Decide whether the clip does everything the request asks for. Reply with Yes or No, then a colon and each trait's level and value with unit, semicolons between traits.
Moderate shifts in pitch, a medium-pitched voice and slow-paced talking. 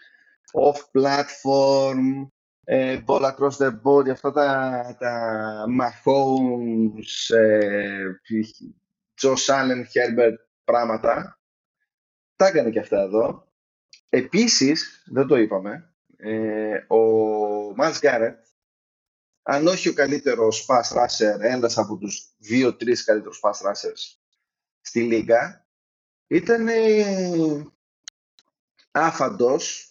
No: average, 4.5 semitones; low, 130 Hz; slow, 90 wpm